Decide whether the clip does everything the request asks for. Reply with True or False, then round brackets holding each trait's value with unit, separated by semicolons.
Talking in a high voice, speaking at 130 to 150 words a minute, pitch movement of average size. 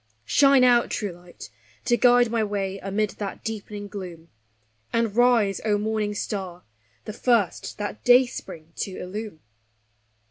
True (210 Hz; 135 wpm; 3.2 semitones)